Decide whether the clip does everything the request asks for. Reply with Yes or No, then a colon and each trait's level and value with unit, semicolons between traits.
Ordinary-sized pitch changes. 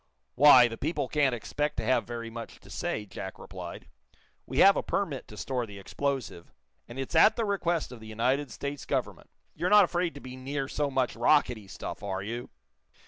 Yes: average, 4.3 semitones